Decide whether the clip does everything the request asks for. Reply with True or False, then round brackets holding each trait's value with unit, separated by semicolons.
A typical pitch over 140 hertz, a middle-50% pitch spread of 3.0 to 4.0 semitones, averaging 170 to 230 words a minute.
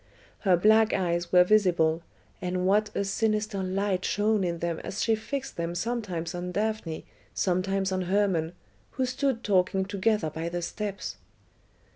False (190 Hz; 3.3 semitones; 150 wpm)